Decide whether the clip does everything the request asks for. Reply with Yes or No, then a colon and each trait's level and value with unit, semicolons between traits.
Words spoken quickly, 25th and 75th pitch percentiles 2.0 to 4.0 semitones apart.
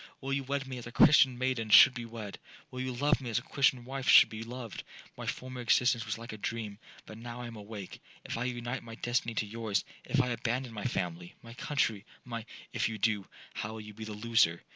Yes: fast, 220 wpm; average, 2.7 semitones